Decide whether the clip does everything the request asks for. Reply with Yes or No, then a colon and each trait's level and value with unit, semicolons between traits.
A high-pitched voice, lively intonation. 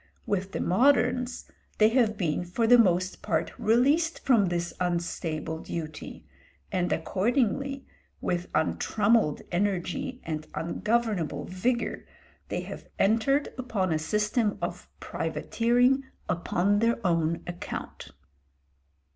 Yes: high, 205 Hz; wide, 5.8 semitones